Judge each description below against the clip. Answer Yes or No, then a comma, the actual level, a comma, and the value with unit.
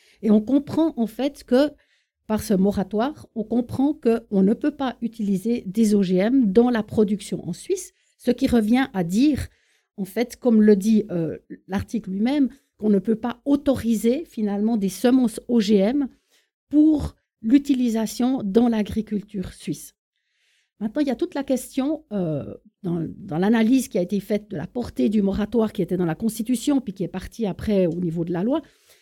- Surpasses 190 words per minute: No, average, 180 wpm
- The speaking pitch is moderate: No, high, 225 Hz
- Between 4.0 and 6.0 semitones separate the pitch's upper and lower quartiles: Yes, average, 4.4 semitones